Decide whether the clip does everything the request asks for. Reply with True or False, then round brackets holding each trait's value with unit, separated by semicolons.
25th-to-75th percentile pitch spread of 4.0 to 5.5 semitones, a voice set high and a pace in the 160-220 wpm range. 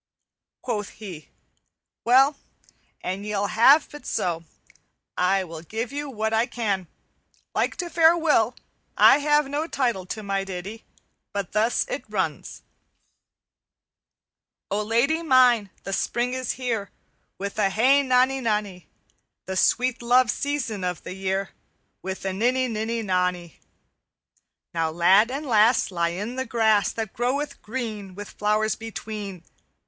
False (4.7 semitones; 220 Hz; 140 wpm)